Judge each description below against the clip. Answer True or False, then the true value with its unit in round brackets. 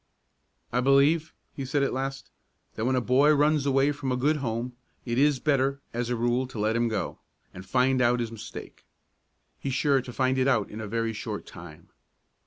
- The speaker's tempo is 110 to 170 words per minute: False (200 wpm)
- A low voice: True (130 Hz)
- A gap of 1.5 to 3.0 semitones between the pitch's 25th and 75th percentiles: True (2.7 semitones)